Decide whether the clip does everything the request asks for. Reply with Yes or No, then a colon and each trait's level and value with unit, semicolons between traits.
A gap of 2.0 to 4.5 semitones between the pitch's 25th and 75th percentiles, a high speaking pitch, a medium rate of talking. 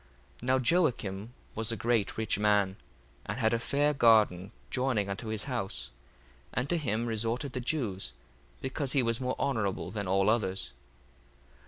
No: average, 4.0 semitones; low, 115 Hz; average, 160 wpm